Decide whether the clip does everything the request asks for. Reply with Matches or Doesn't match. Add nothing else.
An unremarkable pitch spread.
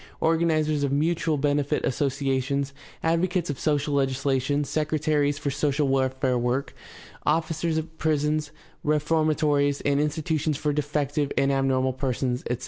Doesn't match